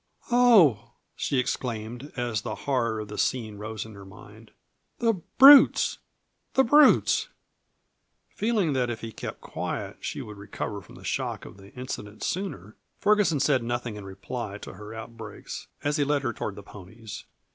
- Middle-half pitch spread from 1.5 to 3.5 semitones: No, wide, 5.6 semitones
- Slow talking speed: No, average, 165 wpm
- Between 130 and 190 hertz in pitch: No, low, 120 Hz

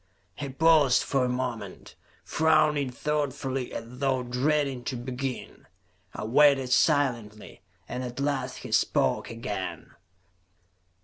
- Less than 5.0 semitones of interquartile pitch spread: Yes, narrow, 2.6 semitones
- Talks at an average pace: No, slow, 115 wpm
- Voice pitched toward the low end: Yes, low, 130 Hz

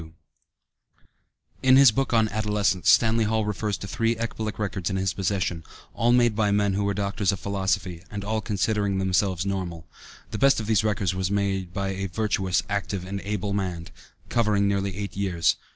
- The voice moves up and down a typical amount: No, narrow, 2.1 semitones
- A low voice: Yes, low, 100 Hz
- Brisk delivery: No, average, 180 wpm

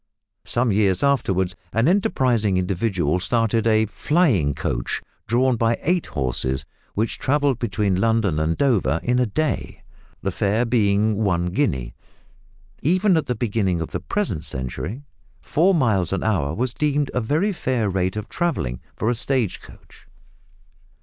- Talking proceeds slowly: No, average, 150 wpm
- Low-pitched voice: Yes, low, 110 Hz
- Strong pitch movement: Yes, wide, 5.9 semitones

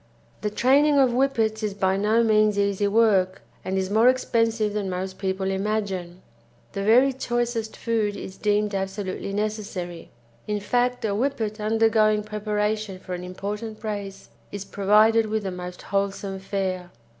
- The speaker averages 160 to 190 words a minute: No, average, 150 wpm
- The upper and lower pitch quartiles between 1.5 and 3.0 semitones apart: Yes, narrow, 2.4 semitones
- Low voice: No, high, 210 Hz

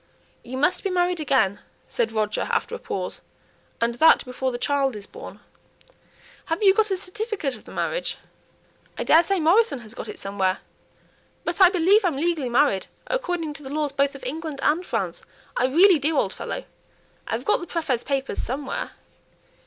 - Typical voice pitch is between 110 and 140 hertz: No, very high, 300 Hz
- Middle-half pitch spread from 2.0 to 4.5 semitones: No, wide, 5.7 semitones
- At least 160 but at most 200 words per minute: Yes, average, 175 wpm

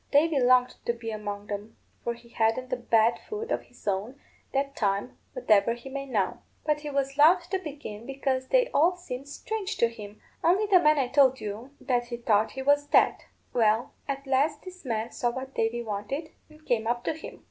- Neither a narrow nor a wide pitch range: Yes, average, 4.4 semitones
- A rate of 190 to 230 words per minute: Yes, average, 200 wpm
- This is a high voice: Yes, very high, 255 Hz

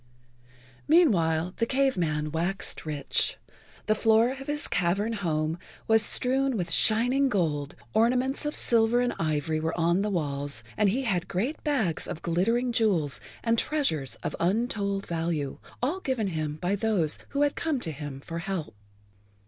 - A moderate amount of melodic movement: No, wide, 7.1 semitones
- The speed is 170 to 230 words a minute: No, average, 160 wpm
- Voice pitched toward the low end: No, high, 195 Hz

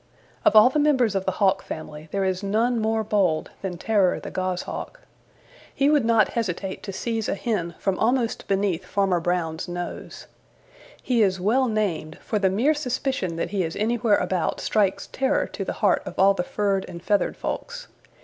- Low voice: No, high, 200 Hz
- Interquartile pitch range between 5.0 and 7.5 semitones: No, average, 3.8 semitones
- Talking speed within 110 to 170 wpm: No, average, 185 wpm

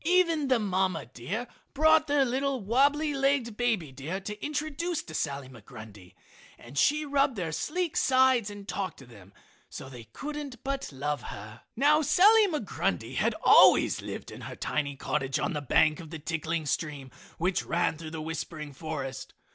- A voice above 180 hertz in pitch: Yes, high, 190 Hz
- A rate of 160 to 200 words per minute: Yes, average, 170 wpm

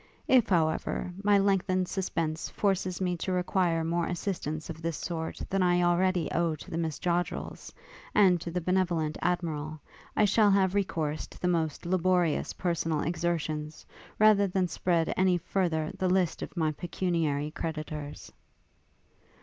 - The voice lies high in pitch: No, medium, 175 Hz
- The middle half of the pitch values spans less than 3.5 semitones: Yes, narrow, 2.6 semitones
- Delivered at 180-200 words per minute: No, average, 150 wpm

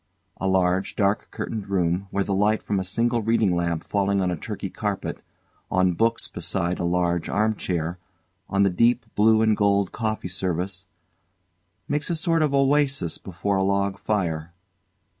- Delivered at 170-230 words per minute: No, average, 160 wpm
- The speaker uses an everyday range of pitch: Yes, average, 3.4 semitones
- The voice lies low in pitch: Yes, low, 100 Hz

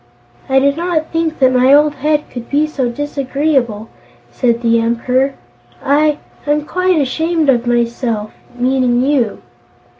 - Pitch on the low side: No, very high, 270 Hz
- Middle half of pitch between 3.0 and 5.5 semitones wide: Yes, average, 3.8 semitones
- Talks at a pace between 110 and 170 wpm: Yes, average, 140 wpm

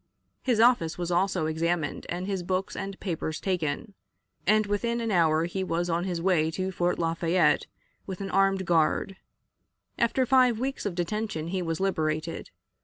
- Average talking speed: Yes, average, 165 wpm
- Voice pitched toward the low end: No, medium, 185 Hz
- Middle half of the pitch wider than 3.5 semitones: No, average, 3.0 semitones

